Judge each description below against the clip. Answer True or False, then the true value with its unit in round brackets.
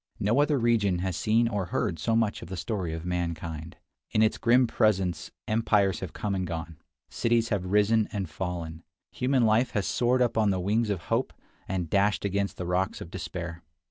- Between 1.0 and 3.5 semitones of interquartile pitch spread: False (4.2 semitones)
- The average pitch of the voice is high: False (100 Hz)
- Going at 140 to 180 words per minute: False (195 wpm)